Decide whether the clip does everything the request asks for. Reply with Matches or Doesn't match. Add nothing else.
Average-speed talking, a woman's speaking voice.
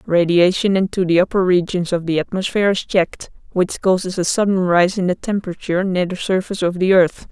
Matches